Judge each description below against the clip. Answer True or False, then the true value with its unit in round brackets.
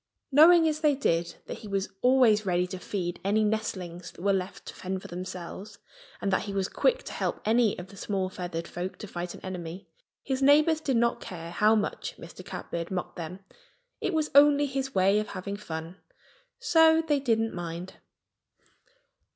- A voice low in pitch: False (200 Hz)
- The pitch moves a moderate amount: False (6.6 semitones)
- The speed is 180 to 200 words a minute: True (185 wpm)